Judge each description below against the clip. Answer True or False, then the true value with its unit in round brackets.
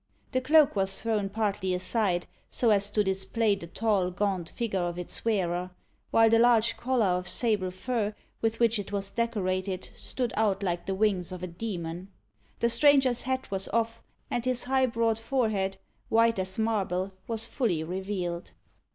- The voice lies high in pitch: True (205 Hz)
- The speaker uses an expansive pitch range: False (3.7 semitones)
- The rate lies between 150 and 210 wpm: True (170 wpm)